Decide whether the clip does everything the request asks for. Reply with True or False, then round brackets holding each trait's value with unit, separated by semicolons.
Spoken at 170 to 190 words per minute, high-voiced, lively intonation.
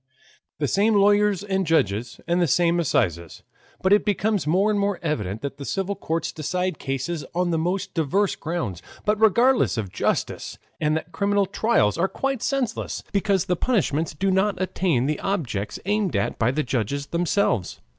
False (175 wpm; 175 Hz; 6.0 semitones)